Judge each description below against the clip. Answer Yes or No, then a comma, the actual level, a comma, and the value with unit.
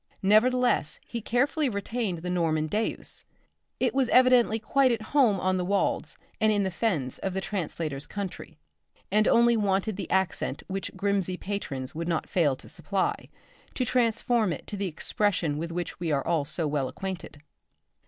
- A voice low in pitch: No, high, 195 Hz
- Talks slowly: No, average, 165 wpm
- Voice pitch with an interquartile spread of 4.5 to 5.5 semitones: Yes, average, 4.8 semitones